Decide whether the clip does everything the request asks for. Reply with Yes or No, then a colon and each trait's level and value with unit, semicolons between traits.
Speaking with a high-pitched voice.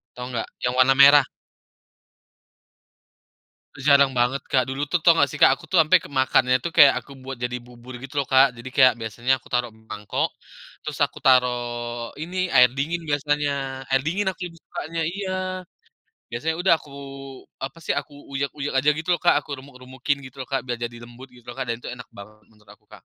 No: low, 135 Hz